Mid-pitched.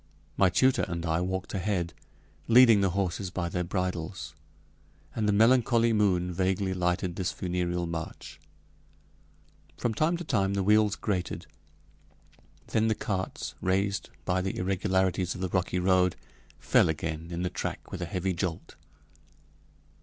No: very low, 95 Hz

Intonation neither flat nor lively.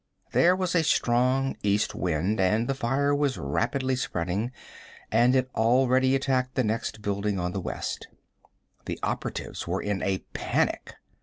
Yes: average, 4.6 semitones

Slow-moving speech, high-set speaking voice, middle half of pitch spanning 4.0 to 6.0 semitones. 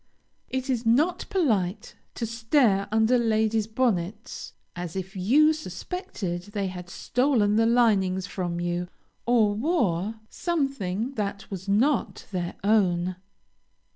Yes: slow, 120 wpm; high, 215 Hz; average, 4.9 semitones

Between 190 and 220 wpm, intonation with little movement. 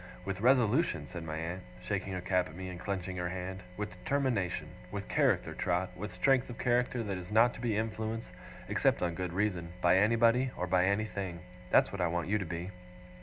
No: fast, 205 wpm; average, 3.7 semitones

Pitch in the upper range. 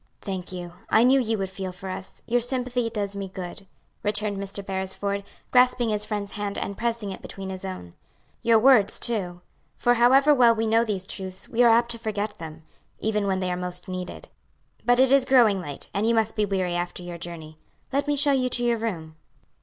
Yes: high, 205 Hz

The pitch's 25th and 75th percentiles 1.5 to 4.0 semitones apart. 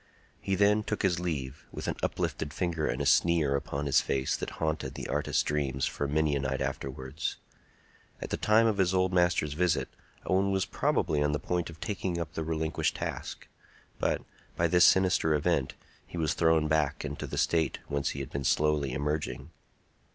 Yes: average, 3.7 semitones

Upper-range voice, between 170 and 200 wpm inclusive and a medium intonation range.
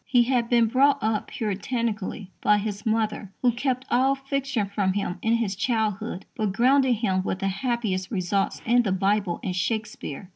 Yes: high, 220 Hz; average, 175 wpm; average, 3.7 semitones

